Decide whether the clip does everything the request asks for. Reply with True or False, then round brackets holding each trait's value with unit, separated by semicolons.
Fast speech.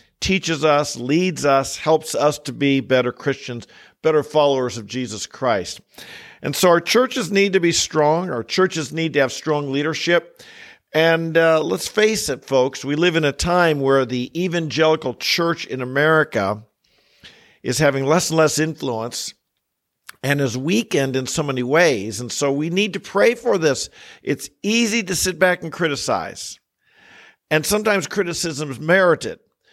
False (160 wpm)